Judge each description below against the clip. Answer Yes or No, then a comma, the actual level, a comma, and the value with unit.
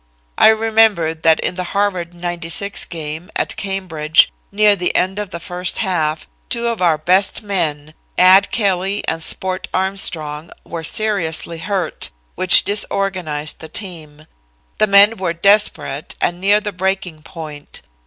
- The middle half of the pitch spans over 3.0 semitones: Yes, average, 3.6 semitones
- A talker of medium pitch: Yes, medium, 180 Hz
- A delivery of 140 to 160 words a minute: Yes, average, 145 wpm